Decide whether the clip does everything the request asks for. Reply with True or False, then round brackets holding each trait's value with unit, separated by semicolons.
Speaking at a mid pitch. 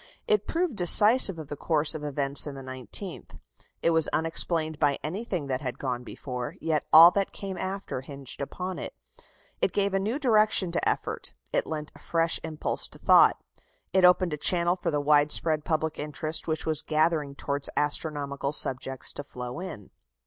True (155 Hz)